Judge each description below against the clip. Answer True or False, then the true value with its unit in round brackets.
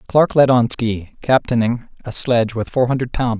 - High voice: False (120 Hz)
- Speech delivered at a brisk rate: False (195 wpm)